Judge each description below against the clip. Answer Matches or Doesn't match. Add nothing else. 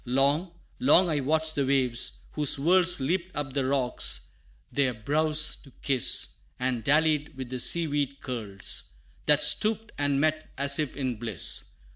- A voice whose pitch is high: Doesn't match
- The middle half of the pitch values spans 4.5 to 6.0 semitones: Doesn't match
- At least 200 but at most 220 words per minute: Doesn't match